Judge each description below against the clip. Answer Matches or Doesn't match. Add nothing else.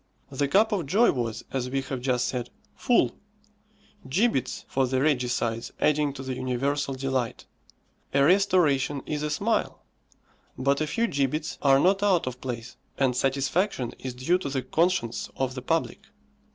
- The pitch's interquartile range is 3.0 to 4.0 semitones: Matches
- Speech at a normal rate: Matches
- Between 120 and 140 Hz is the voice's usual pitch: Matches